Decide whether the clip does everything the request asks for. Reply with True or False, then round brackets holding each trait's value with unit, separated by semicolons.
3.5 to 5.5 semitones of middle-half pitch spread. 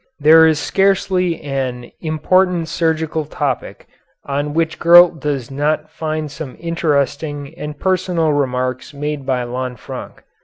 False (3.0 semitones)